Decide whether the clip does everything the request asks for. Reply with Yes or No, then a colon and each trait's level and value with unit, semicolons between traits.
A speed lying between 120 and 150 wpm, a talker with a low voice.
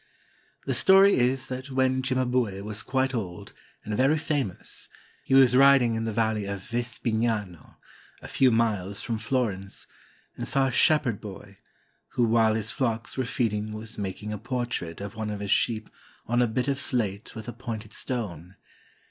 No: average, 175 wpm; low, 115 Hz